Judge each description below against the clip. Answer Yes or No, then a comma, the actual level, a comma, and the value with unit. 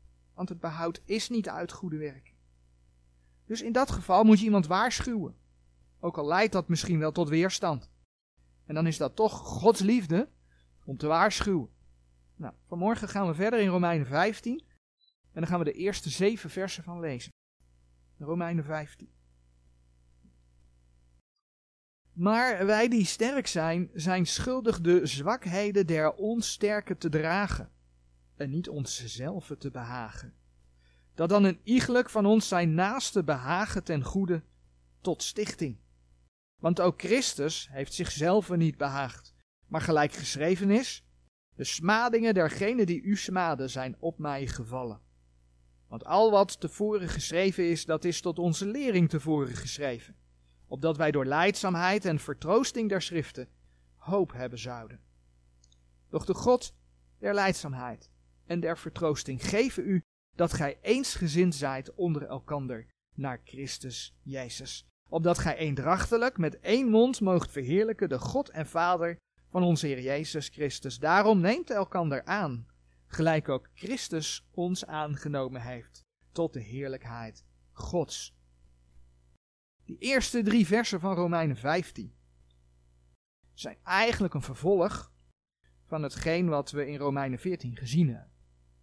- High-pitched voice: No, medium, 155 Hz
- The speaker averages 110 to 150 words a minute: Yes, slow, 135 wpm